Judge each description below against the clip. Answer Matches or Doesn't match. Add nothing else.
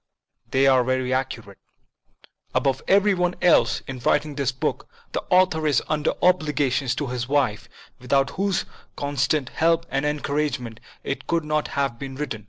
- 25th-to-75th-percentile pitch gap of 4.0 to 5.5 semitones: Doesn't match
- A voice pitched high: Doesn't match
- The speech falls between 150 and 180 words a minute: Matches